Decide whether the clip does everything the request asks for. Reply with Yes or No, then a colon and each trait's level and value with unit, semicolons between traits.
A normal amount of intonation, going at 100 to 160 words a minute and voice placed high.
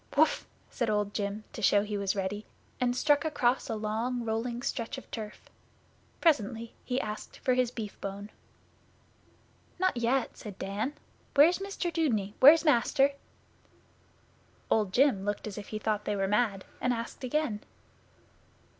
Yes: average, 4.0 semitones; average, 145 wpm; high, 230 Hz